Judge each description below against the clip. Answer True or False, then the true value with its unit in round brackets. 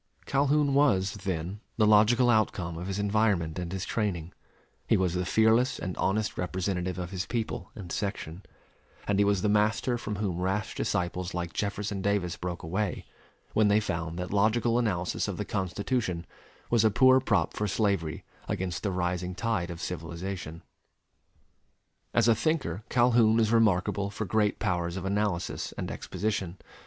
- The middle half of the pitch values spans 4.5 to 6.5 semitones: False (3.4 semitones)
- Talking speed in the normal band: True (160 wpm)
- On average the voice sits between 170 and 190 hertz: False (100 Hz)